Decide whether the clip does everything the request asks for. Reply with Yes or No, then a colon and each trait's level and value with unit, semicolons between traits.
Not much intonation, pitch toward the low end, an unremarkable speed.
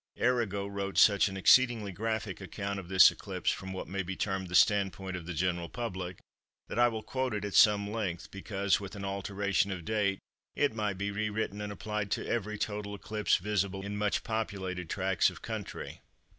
Yes: narrow, 1.8 semitones; low, 100 Hz; average, 195 wpm